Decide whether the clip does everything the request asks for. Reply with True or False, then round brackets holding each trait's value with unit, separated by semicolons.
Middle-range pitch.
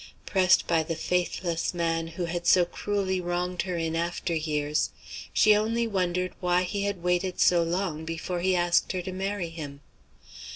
True (175 Hz)